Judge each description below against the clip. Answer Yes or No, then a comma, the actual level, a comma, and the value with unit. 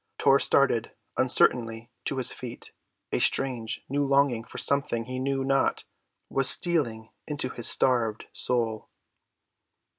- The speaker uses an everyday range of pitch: Yes, average, 3.0 semitones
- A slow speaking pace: Yes, slow, 125 wpm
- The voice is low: Yes, low, 130 Hz